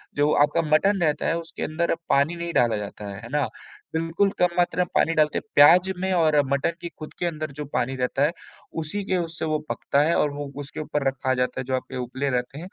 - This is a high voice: No, medium, 155 Hz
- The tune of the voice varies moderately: Yes, average, 3.6 semitones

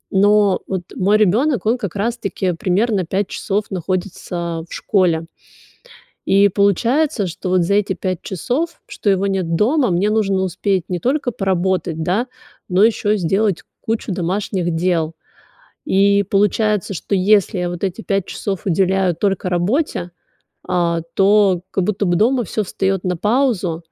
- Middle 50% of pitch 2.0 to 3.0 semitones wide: Yes, average, 2.7 semitones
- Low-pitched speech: No, high, 195 Hz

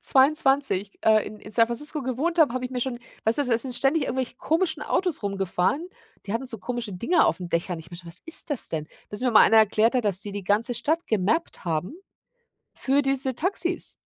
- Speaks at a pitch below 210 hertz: No, high, 240 Hz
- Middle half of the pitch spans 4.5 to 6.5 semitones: Yes, wide, 5.6 semitones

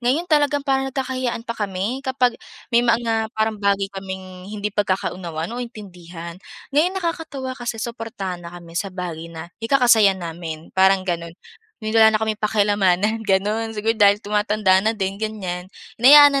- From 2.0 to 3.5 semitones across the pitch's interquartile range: No, average, 4.1 semitones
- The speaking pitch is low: No, high, 210 Hz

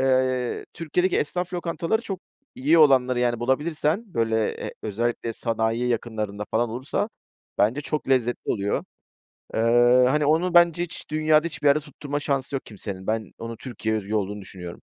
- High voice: No, low, 130 Hz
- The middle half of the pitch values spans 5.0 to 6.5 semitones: Yes, wide, 5.6 semitones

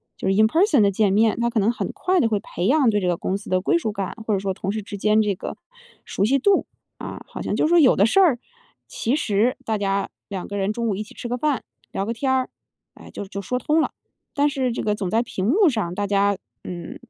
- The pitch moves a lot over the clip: No, average, 4.5 semitones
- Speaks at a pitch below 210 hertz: No, high, 215 Hz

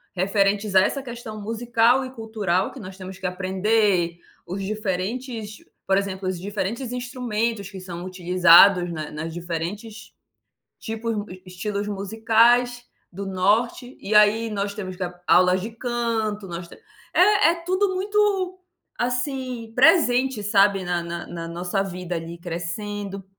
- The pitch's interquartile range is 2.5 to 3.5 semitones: No, average, 3.9 semitones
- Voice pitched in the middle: No, high, 205 Hz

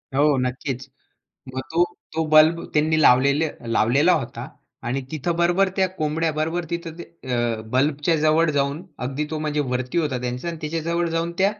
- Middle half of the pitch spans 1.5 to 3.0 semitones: No, average, 3.6 semitones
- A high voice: No, medium, 155 Hz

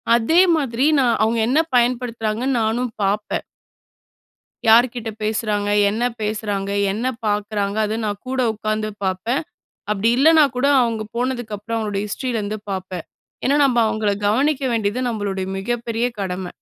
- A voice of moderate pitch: No, high, 220 Hz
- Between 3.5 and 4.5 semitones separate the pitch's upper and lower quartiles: No, average, 2.8 semitones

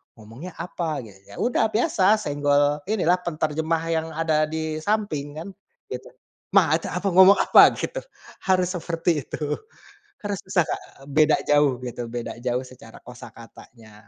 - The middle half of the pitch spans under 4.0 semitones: No, average, 4.6 semitones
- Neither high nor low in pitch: Yes, medium, 155 Hz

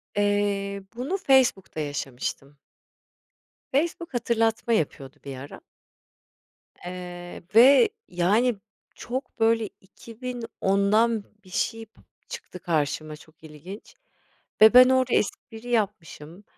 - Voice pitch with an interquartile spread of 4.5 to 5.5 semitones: Yes, average, 5.2 semitones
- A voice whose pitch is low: No, high, 205 Hz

